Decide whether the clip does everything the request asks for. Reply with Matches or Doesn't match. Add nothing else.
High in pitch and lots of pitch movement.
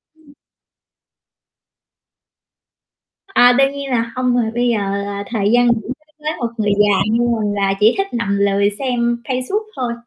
Doesn't match